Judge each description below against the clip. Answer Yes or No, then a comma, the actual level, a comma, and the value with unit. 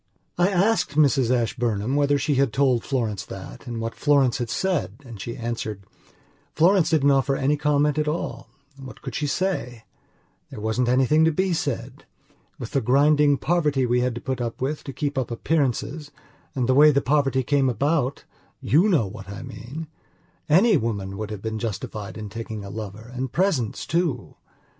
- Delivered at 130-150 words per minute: No, average, 170 wpm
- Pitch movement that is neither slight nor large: Yes, average, 4.4 semitones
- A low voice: Yes, low, 130 Hz